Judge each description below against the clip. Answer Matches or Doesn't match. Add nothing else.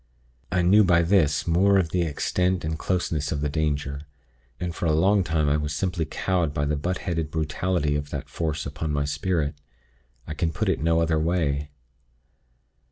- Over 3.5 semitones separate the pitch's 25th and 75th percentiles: Doesn't match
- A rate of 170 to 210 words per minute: Matches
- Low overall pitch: Matches